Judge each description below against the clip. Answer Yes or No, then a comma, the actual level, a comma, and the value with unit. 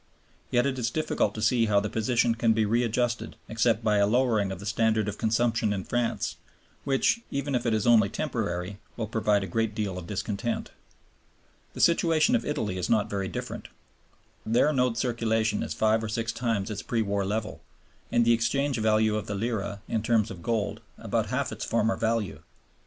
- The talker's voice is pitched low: Yes, low, 110 Hz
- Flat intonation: Yes, narrow, 2.3 semitones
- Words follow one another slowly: No, average, 195 wpm